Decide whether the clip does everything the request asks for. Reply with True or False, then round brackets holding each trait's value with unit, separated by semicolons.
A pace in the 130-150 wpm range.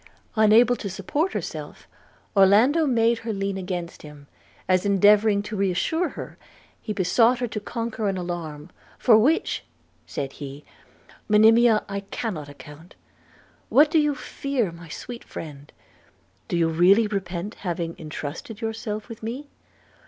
True (140 wpm)